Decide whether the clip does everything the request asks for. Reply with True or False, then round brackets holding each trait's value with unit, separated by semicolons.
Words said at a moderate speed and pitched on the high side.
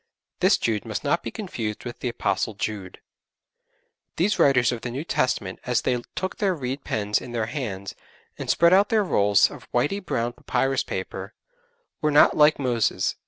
False (175 wpm; 125 Hz)